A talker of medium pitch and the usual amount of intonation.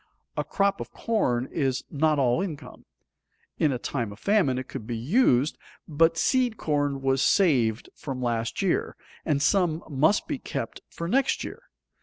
No: medium, 145 Hz; wide, 6.2 semitones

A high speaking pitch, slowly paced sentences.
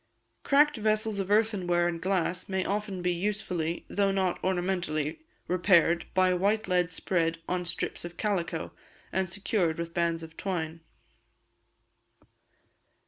No: medium, 180 Hz; slow, 130 wpm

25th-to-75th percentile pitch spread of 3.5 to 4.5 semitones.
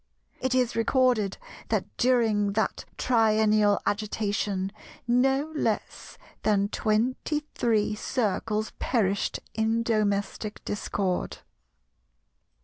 No: average, 2.8 semitones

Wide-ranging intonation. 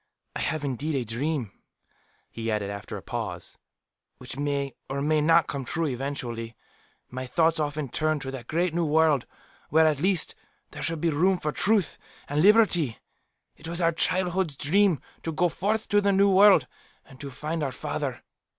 No: average, 4.0 semitones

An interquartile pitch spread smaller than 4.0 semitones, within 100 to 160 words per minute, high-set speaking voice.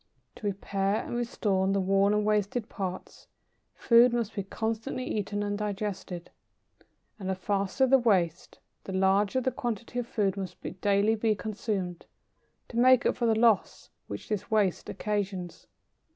Yes: average, 2.8 semitones; average, 155 wpm; high, 205 Hz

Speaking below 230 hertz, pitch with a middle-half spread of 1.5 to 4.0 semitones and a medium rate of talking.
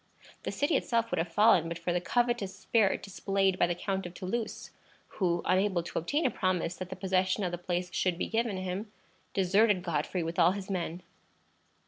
Yes: medium, 185 Hz; narrow, 2.5 semitones; average, 195 wpm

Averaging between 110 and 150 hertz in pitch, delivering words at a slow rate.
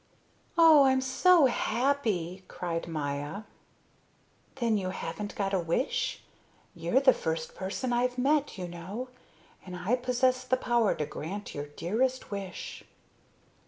No: high, 215 Hz; slow, 130 wpm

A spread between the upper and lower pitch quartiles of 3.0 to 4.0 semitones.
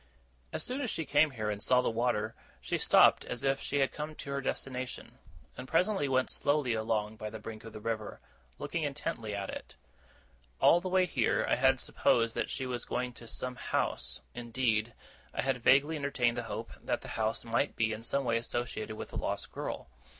Yes: average, 3.7 semitones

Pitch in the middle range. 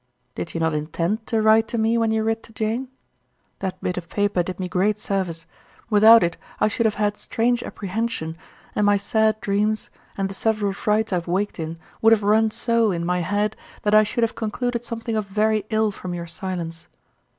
No: high, 210 Hz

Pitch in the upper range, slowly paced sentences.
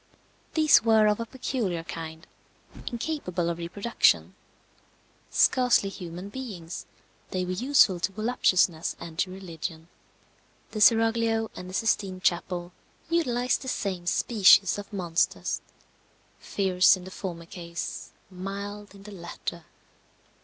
Yes: high, 195 Hz; slow, 120 wpm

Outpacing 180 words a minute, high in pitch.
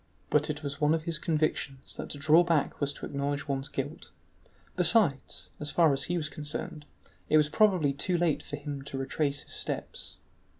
No: average, 195 wpm; medium, 150 Hz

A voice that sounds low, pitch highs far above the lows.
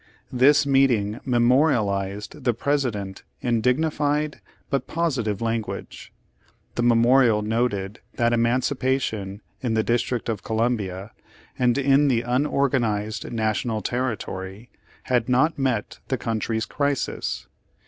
No: low, 120 Hz; average, 3.6 semitones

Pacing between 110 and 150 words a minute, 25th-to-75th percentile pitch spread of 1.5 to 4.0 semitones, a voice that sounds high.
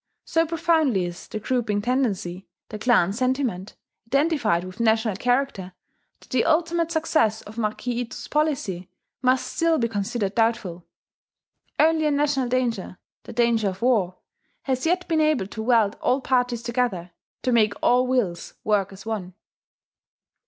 No: average, 145 wpm; average, 4.8 semitones; high, 235 Hz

